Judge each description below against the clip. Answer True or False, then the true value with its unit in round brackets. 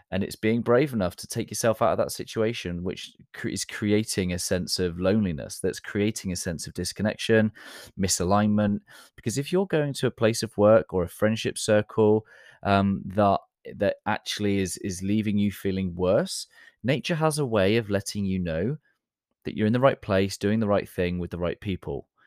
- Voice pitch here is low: True (105 Hz)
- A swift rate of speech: False (190 wpm)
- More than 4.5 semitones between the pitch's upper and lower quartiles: False (3.1 semitones)